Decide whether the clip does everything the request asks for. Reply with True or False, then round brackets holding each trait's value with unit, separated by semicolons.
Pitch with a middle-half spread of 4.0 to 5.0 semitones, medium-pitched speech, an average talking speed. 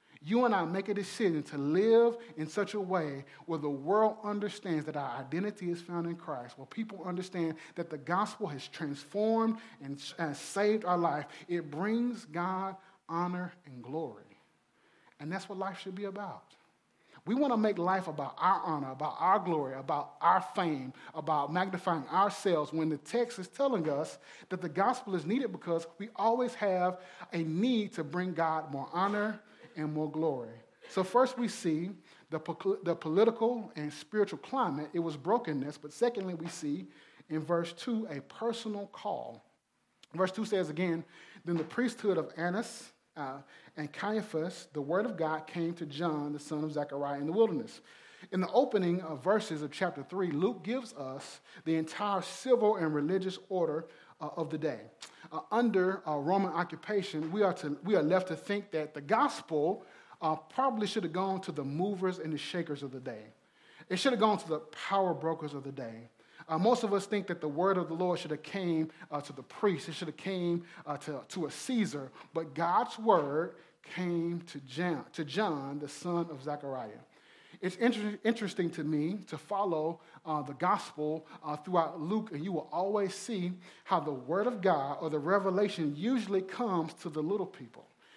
True (4.6 semitones; 175 Hz; 185 wpm)